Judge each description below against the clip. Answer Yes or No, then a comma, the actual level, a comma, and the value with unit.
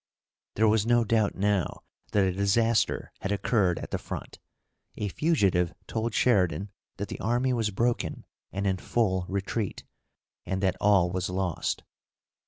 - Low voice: Yes, low, 100 Hz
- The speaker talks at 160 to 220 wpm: No, average, 150 wpm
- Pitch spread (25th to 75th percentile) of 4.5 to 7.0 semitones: No, average, 3.2 semitones